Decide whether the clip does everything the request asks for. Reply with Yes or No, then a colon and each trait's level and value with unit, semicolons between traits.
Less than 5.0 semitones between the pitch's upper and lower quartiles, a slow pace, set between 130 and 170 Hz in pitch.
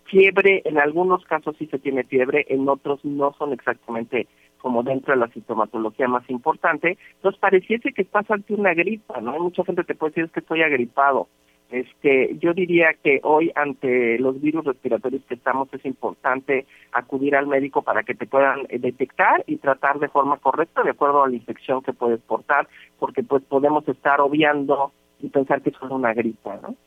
No: average, 3.8 semitones; average, 185 wpm; medium, 140 Hz